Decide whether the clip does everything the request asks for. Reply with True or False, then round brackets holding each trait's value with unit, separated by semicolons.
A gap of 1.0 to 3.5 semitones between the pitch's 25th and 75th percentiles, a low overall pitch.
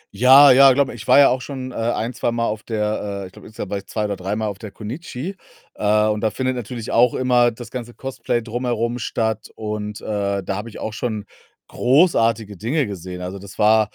True (2.9 semitones; 110 Hz)